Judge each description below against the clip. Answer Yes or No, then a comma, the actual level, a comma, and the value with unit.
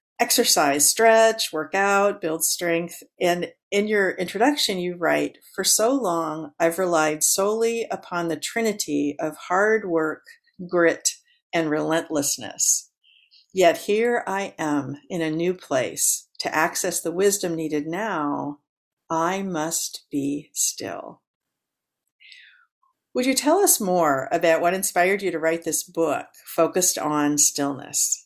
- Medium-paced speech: No, slow, 130 wpm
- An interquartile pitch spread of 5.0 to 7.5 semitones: No, average, 4.4 semitones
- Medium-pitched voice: Yes, medium, 175 Hz